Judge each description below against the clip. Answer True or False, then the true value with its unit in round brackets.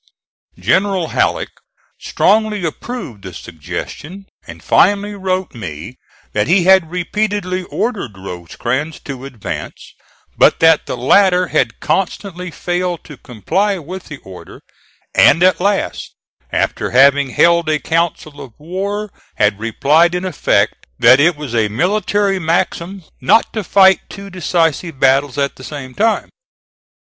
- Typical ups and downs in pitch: False (6.2 semitones)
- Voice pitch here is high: False (170 Hz)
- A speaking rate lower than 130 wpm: False (135 wpm)